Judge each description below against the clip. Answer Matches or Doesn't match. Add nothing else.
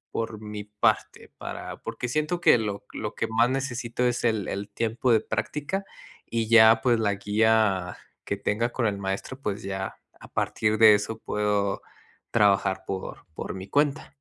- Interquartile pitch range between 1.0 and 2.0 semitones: Doesn't match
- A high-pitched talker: Doesn't match